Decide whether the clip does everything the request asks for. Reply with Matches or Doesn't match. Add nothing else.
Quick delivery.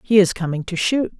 Matches